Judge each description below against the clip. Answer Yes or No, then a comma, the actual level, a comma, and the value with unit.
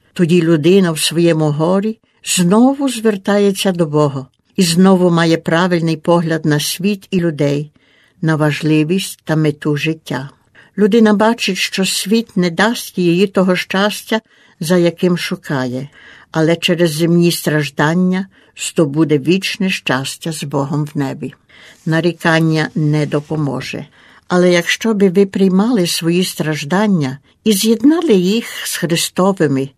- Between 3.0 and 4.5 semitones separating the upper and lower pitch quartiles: Yes, average, 4.0 semitones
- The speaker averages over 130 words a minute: No, average, 125 wpm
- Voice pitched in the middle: Yes, medium, 170 Hz